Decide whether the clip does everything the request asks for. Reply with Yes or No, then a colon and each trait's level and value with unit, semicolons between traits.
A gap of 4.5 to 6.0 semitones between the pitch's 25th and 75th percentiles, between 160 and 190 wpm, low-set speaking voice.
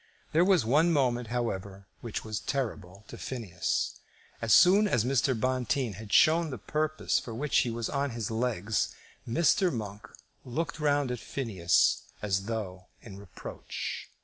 No: average, 5.3 semitones; average, 150 wpm; low, 120 Hz